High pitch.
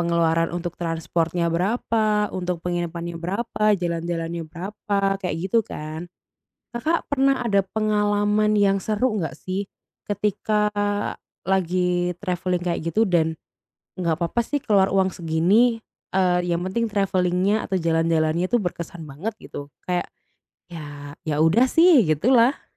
No: medium, 180 Hz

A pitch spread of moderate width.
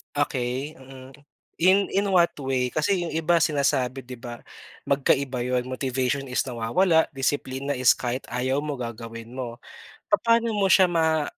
Yes: average, 4.3 semitones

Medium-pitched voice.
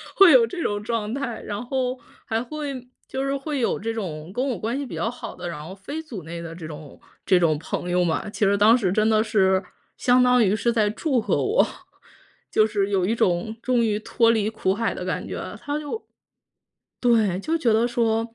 No: high, 225 Hz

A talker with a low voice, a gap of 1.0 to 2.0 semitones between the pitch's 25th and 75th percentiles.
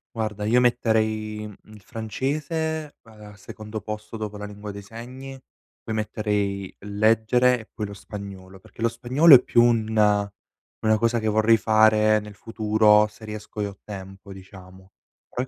Yes: low, 110 Hz; narrow, 1.7 semitones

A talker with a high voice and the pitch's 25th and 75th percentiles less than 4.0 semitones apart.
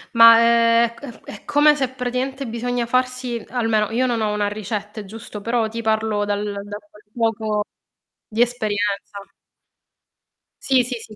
Yes: high, 230 Hz; narrow, 2.6 semitones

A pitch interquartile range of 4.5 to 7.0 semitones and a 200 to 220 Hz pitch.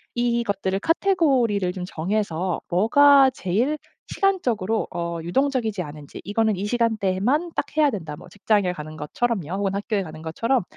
Yes: average, 5.3 semitones; high, 205 Hz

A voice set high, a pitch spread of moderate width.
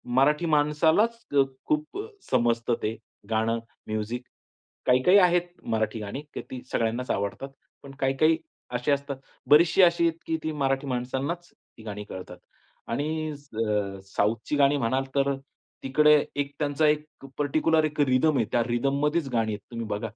No: low, 135 Hz; average, 4.7 semitones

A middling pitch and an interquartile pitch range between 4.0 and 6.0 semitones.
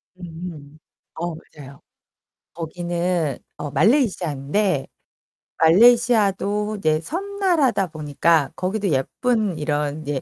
Yes: medium, 170 Hz; wide, 5.6 semitones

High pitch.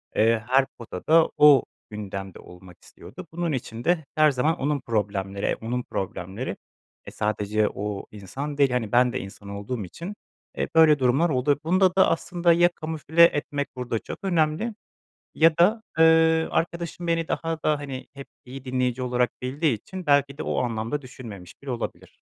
No: low, 135 Hz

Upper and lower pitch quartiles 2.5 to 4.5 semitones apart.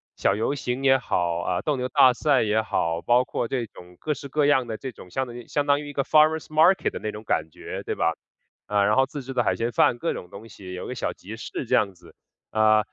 No: average, 4.9 semitones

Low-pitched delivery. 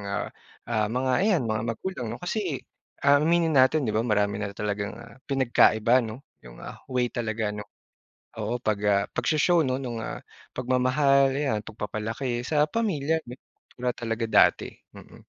Yes: low, 125 Hz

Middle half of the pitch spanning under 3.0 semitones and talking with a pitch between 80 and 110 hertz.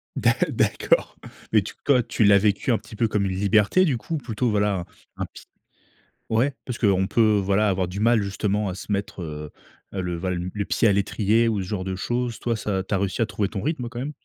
No: average, 3.3 semitones; low, 105 Hz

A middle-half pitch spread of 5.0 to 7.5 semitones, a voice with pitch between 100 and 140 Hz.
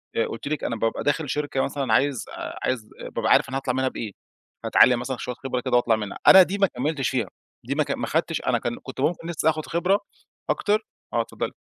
No: average, 4.2 semitones; low, 135 Hz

